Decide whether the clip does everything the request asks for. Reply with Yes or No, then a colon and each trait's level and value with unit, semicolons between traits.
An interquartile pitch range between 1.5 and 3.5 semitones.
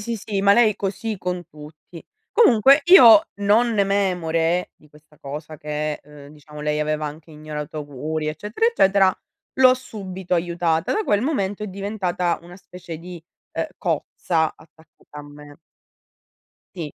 No: average, 4.8 semitones